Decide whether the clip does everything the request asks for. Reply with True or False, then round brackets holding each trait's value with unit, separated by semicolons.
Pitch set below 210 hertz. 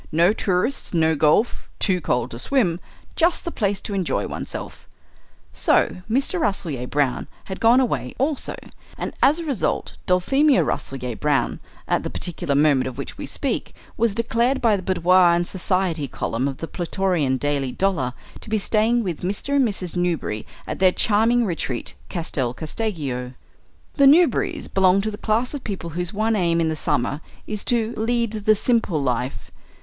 True (185 Hz)